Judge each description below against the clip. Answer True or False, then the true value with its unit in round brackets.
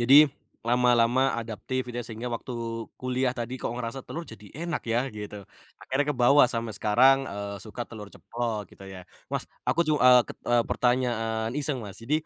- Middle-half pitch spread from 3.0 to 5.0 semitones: False (2.5 semitones)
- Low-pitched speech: True (120 Hz)